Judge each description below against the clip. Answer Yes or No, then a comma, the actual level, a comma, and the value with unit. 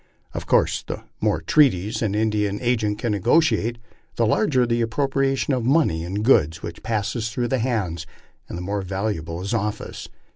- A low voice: Yes, low, 110 Hz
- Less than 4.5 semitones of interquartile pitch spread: Yes, average, 3.8 semitones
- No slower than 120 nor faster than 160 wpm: No, average, 175 wpm